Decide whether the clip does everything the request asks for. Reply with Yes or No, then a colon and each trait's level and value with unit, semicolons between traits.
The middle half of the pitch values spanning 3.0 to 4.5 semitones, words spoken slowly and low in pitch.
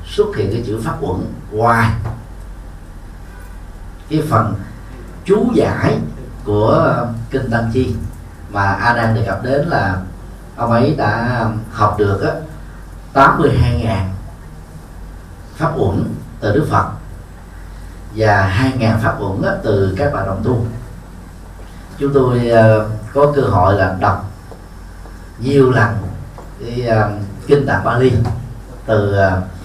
Yes: average, 4.0 semitones; slow, 120 wpm; low, 105 Hz